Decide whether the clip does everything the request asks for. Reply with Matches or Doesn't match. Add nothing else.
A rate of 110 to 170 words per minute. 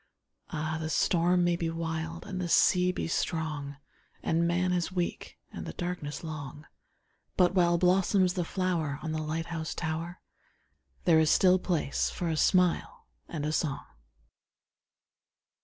Matches